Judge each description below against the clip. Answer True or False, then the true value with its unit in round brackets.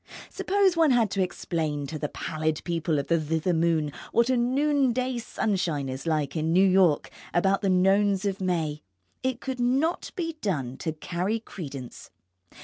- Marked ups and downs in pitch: True (7.3 semitones)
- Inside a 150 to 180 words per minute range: True (165 wpm)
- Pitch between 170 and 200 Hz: True (185 Hz)